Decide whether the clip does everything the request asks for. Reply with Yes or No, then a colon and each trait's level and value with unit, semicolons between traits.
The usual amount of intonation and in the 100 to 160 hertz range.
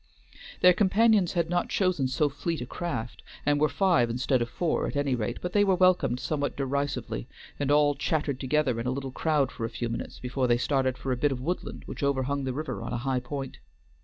Yes: average, 4.0 semitones; medium, 140 Hz